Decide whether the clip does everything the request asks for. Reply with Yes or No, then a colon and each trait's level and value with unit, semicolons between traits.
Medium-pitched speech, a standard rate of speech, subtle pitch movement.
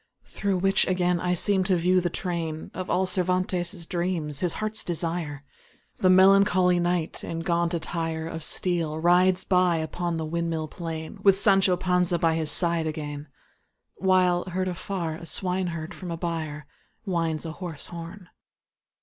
Yes: medium, 175 Hz; average, 155 wpm; narrow, 2.1 semitones